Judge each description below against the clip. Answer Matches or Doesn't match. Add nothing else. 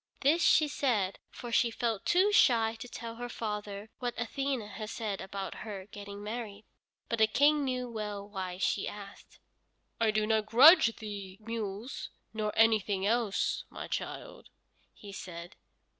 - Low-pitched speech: Doesn't match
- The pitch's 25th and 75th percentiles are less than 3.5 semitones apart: Matches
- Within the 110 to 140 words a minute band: Doesn't match